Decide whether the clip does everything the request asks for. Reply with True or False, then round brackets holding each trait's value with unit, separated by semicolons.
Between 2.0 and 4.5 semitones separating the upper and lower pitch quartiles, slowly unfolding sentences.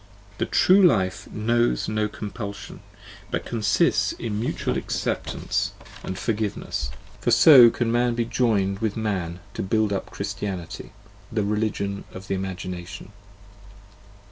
True (2.9 semitones; 130 wpm)